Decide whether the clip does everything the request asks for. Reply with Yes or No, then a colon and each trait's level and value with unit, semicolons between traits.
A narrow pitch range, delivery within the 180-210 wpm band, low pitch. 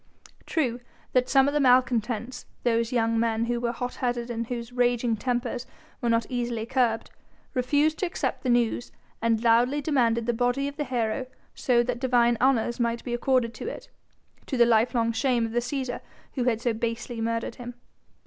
No: narrow, 1.6 semitones; average, 185 wpm; high, 240 Hz